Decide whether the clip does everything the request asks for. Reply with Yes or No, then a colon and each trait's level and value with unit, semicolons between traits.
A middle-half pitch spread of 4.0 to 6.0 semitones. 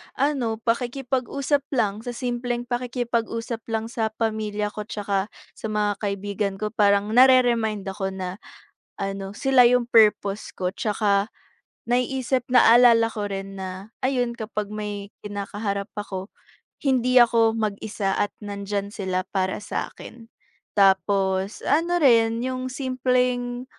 No: average, 3.5 semitones